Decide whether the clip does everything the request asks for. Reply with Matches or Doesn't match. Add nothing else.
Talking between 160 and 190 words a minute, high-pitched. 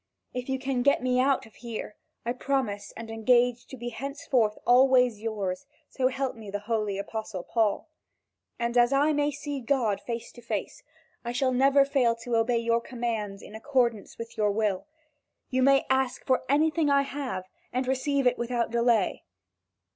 Matches